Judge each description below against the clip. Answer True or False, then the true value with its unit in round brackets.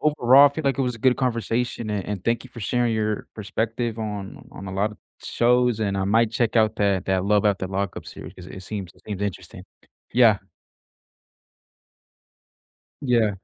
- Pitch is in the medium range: False (110 Hz)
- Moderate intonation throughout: True (3.3 semitones)